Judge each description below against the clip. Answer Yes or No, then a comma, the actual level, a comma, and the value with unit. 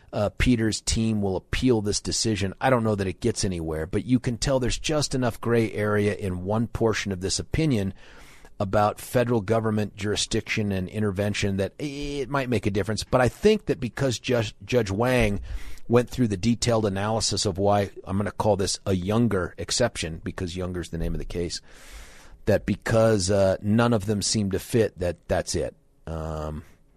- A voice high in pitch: No, low, 105 Hz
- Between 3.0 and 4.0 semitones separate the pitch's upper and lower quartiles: Yes, average, 3.5 semitones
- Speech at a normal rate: Yes, average, 190 wpm